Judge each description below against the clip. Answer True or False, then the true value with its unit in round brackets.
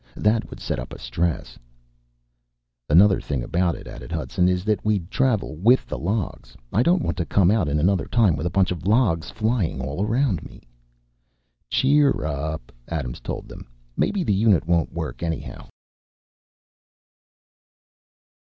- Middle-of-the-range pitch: False (90 Hz)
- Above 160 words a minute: False (155 wpm)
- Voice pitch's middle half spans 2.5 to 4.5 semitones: False (5.2 semitones)